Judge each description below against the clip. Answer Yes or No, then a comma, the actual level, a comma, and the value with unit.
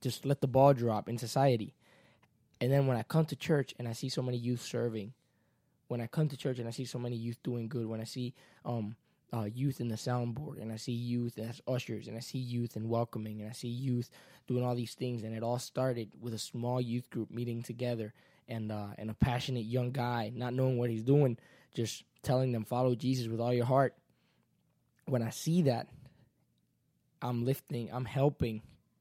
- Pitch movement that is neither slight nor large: No, narrow, 2.0 semitones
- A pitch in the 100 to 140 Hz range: Yes, low, 120 Hz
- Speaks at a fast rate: Yes, fast, 215 wpm